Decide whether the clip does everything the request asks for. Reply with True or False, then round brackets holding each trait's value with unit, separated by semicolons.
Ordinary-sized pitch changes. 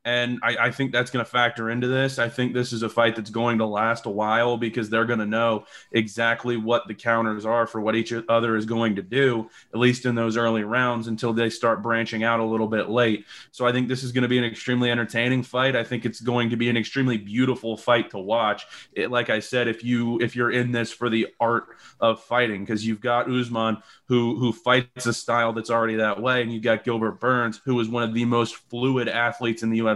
False (1.3 semitones)